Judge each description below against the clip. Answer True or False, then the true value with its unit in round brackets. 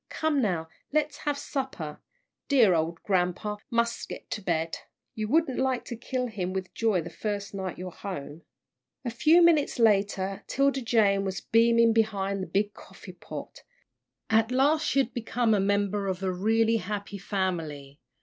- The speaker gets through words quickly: False (165 wpm)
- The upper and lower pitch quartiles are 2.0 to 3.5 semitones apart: False (4.2 semitones)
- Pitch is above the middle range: True (210 Hz)